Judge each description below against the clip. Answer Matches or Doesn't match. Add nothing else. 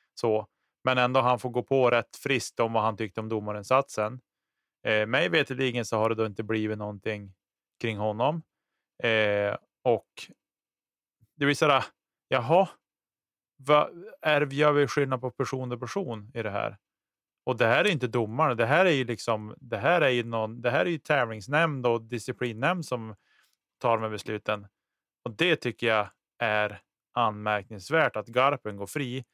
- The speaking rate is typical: Matches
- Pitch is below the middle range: Matches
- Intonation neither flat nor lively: Matches